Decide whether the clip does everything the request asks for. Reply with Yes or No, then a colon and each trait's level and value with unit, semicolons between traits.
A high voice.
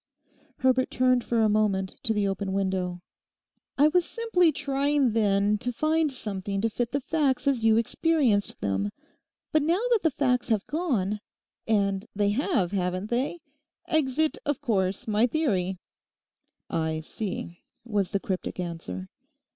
Yes: high, 225 Hz